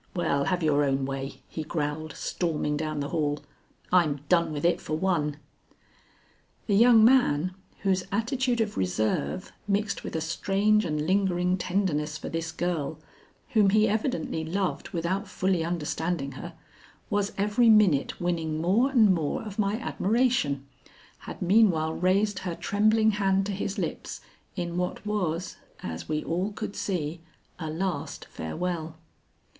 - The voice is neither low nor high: Yes, medium, 180 Hz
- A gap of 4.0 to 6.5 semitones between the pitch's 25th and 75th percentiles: Yes, average, 4.6 semitones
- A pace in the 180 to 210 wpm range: No, average, 145 wpm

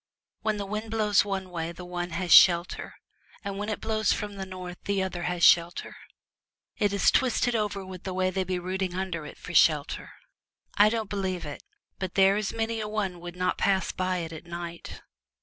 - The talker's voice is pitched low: No, high, 190 Hz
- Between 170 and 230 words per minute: Yes, average, 200 wpm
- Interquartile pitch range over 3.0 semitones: No, average, 2.7 semitones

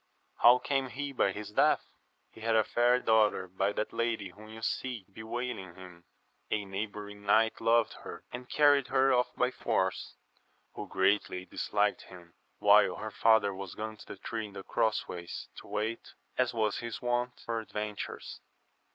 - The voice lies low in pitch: Yes, low, 110 Hz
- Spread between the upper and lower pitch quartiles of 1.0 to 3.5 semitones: Yes, average, 3.1 semitones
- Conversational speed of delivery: Yes, average, 175 wpm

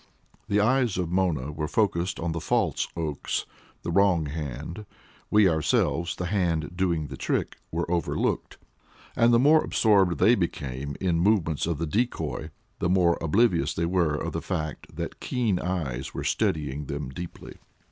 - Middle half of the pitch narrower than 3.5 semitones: No, average, 3.9 semitones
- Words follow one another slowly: No, average, 165 wpm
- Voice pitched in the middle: No, very low, 85 Hz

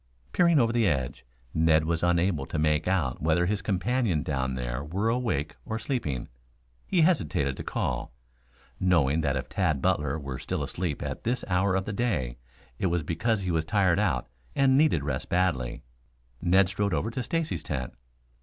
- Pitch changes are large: Yes, wide, 6.4 semitones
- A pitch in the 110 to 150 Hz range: No, very low, 85 Hz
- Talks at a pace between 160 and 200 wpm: Yes, average, 175 wpm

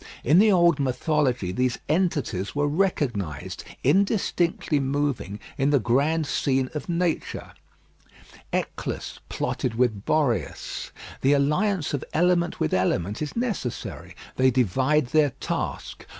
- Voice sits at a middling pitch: Yes, medium, 145 Hz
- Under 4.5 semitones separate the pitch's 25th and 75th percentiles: No, average, 4.9 semitones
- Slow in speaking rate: Yes, slow, 120 wpm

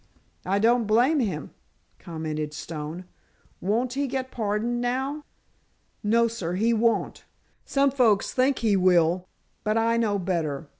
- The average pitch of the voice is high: Yes, high, 220 Hz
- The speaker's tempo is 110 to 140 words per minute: Yes, slow, 135 wpm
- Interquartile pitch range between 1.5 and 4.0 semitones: No, average, 5.2 semitones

